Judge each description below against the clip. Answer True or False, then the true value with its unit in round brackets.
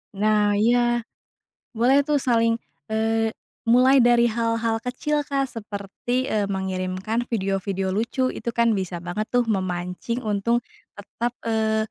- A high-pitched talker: True (225 Hz)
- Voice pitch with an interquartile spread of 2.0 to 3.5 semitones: True (3.1 semitones)